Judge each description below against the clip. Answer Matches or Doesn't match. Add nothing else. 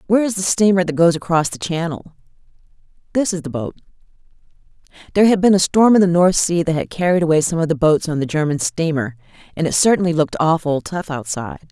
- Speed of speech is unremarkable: Doesn't match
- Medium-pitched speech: Matches